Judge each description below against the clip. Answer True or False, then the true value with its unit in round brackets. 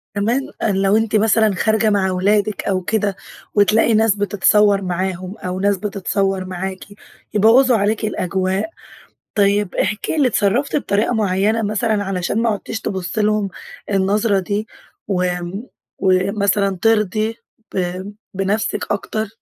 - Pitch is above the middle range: True (205 Hz)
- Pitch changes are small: True (2.2 semitones)